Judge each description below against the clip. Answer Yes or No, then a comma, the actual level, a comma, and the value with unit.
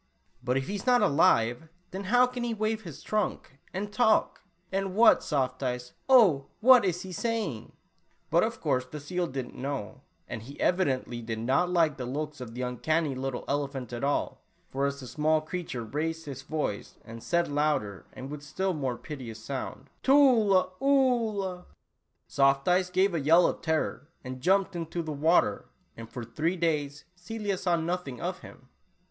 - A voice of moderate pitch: Yes, medium, 155 Hz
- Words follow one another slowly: No, average, 180 wpm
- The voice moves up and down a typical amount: No, wide, 5.9 semitones